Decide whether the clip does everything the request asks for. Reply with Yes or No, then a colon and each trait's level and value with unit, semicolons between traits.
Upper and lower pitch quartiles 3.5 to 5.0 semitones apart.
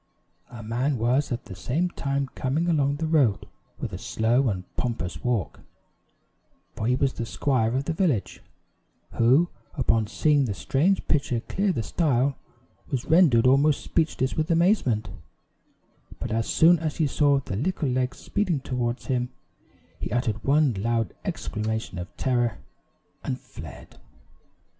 Yes: average, 4.5 semitones